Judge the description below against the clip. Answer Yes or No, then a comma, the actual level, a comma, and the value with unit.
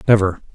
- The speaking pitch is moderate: No, low, 100 Hz